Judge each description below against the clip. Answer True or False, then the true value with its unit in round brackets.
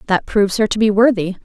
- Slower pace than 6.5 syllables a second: False (6.7 syllables/s)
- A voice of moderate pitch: False (205 Hz)